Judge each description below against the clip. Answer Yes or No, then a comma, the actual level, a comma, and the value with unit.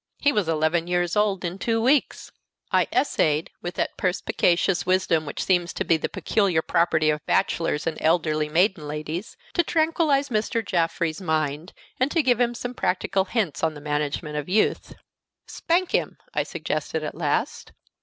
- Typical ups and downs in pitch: No, wide, 5.7 semitones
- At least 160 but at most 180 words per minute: Yes, average, 165 wpm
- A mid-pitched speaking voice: Yes, medium, 175 Hz